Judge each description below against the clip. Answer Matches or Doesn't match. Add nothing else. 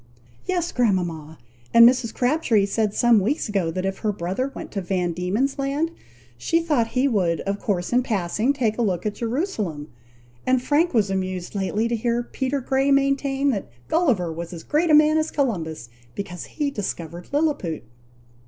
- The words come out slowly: Doesn't match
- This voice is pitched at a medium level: Doesn't match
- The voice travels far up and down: Matches